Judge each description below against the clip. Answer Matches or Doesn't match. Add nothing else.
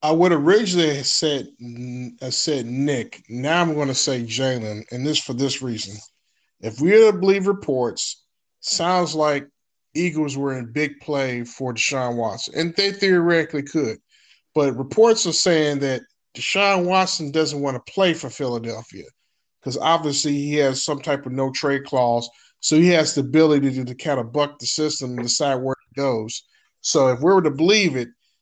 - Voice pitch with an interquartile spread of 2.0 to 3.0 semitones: Doesn't match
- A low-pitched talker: Doesn't match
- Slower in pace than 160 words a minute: Doesn't match